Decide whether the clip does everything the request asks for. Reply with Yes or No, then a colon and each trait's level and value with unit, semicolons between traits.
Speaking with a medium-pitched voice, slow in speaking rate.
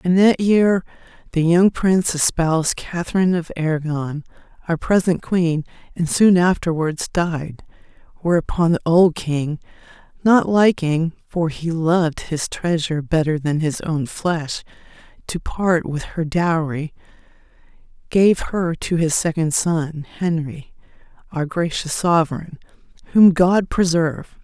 Yes: medium, 165 Hz; slow, 120 wpm